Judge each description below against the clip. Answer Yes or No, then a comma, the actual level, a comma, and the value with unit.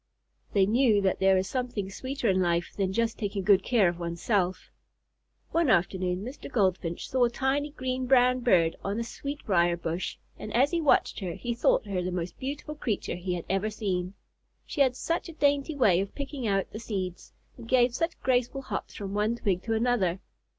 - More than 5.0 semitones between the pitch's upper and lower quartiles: Yes, wide, 5.5 semitones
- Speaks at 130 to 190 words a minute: No, average, 200 wpm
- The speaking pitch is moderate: No, high, 215 Hz